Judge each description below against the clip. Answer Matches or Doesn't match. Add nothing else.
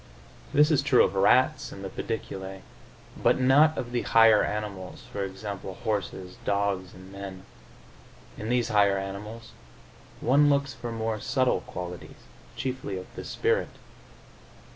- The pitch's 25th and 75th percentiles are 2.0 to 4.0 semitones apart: Doesn't match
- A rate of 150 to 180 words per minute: Doesn't match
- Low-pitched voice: Matches